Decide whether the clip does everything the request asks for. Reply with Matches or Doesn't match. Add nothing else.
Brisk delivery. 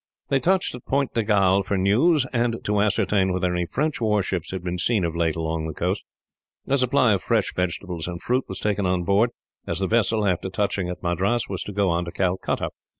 Matches